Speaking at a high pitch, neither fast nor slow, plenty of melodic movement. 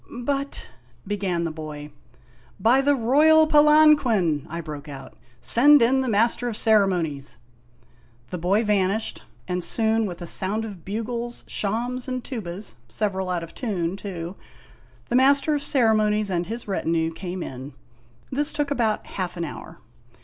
Yes: high, 205 Hz; average, 165 wpm; wide, 6.3 semitones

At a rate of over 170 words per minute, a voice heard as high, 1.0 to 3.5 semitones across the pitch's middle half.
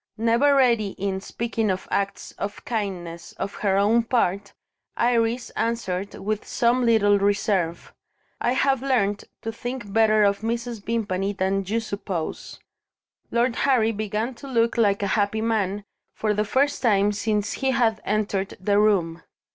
No: average, 150 wpm; high, 215 Hz; average, 2.7 semitones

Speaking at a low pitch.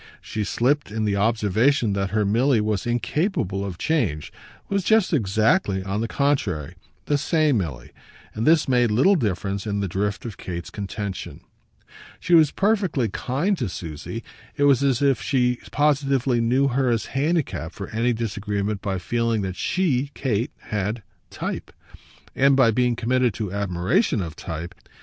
Yes: low, 115 Hz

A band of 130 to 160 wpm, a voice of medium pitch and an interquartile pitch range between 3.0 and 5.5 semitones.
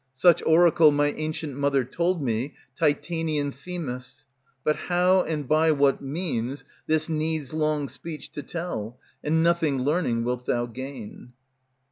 Yes: slow, 135 wpm; medium, 150 Hz; average, 3.5 semitones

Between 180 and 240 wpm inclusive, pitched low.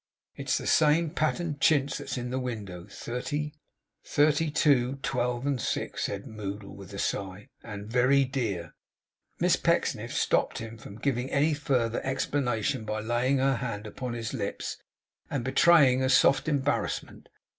No: average, 150 wpm; low, 125 Hz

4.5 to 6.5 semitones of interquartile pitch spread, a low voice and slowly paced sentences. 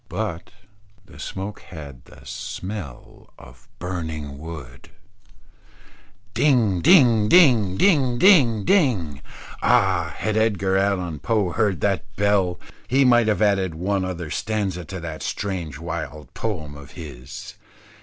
Yes: average, 5.3 semitones; very low, 95 Hz; slow, 125 wpm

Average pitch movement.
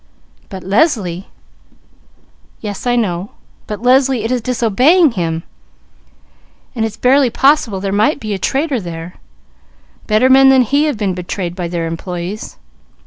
No: wide, 5.9 semitones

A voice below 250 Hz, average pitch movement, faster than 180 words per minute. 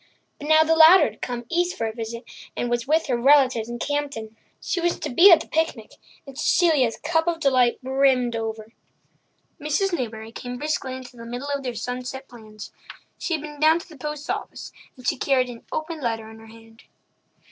No: very high, 260 Hz; average, 4.8 semitones; average, 200 wpm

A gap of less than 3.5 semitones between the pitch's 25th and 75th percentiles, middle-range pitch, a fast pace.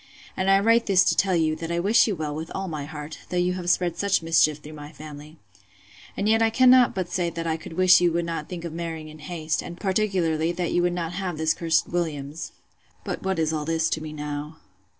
Yes: average, 2.9 semitones; medium, 165 Hz; fast, 235 wpm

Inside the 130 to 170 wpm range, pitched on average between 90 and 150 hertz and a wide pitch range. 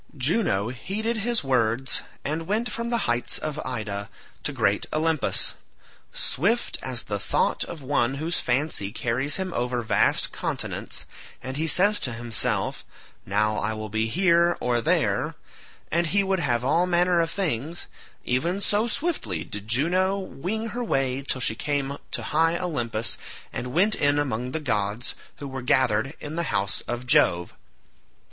Yes: average, 155 wpm; medium, 140 Hz; wide, 6.8 semitones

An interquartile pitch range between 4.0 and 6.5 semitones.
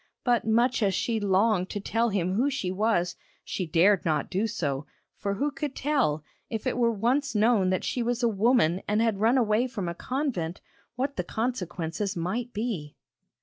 Yes: average, 4.7 semitones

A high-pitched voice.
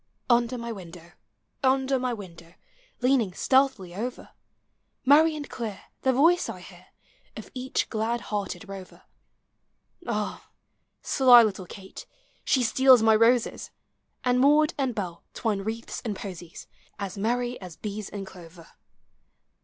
Yes: high, 225 Hz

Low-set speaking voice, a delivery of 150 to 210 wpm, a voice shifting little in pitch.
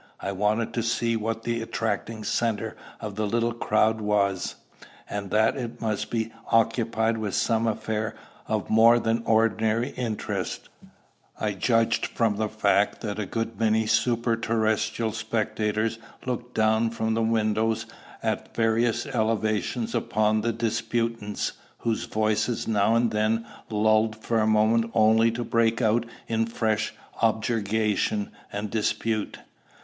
No: low, 110 Hz; slow, 135 wpm; narrow, 1.1 semitones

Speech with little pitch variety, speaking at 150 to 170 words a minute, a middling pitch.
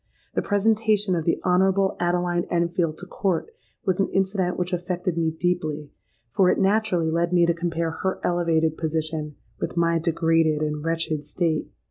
Yes: narrow, 2.2 semitones; average, 160 wpm; medium, 170 Hz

